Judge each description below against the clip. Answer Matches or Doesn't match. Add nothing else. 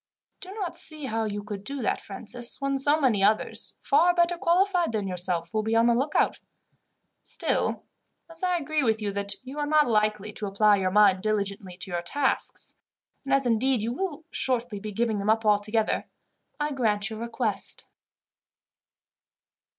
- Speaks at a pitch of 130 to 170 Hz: Doesn't match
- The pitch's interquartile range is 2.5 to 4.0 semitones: Doesn't match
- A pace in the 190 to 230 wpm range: Doesn't match